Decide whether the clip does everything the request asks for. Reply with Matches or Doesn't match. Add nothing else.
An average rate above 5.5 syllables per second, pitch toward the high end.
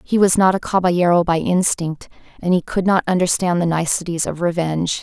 Doesn't match